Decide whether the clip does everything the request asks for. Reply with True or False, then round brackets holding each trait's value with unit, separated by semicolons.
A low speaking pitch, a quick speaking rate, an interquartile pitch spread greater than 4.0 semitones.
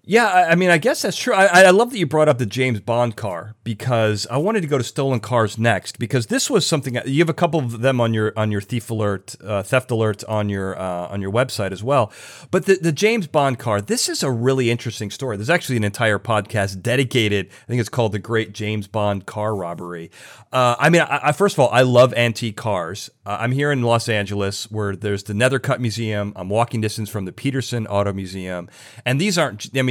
True (115 Hz; 235 wpm; 4.6 semitones)